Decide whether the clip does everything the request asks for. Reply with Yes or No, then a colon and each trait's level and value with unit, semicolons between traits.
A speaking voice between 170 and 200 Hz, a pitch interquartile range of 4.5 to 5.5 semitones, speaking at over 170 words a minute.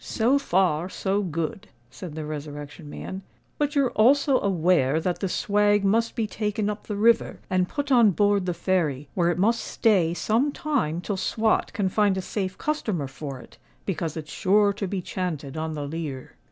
Yes: high, 190 Hz; average, 4.9 semitones; average, 185 wpm